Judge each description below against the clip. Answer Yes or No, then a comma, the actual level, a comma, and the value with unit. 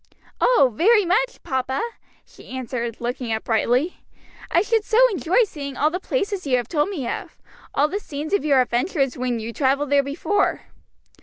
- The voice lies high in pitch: Yes, very high, 285 Hz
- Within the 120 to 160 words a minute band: No, average, 175 wpm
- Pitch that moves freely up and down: Yes, wide, 7.0 semitones